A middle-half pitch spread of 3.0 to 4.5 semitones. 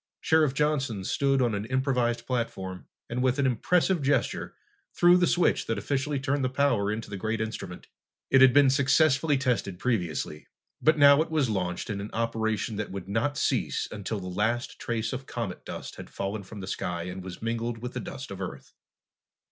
No: average, 5.1 semitones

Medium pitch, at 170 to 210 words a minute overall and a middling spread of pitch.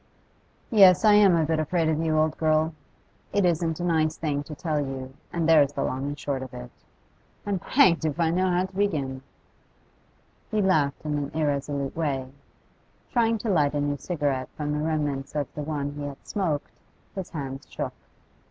Yes: medium, 155 Hz; average, 190 wpm; average, 3.4 semitones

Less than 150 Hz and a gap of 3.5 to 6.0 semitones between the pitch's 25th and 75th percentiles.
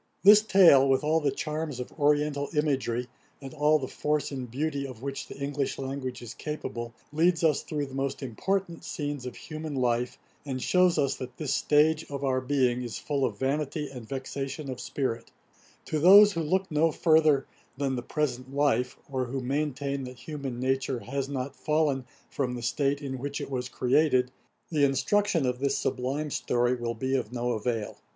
No: medium, 140 Hz; average, 3.0 semitones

